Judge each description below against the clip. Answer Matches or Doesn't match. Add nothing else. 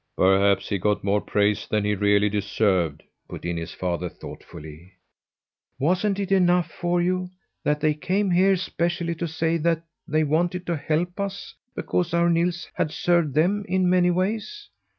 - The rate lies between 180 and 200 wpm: Doesn't match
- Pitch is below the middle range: Doesn't match